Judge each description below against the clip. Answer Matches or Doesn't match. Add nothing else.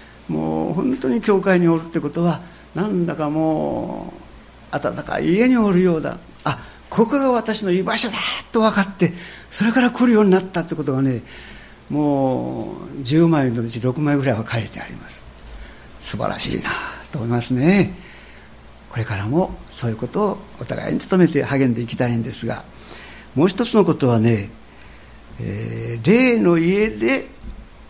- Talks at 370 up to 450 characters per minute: Doesn't match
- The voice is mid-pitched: Matches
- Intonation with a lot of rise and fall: Matches